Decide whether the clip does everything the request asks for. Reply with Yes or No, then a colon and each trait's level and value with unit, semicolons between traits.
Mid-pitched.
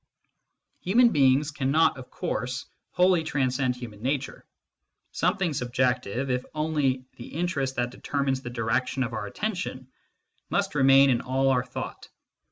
No: low, 130 Hz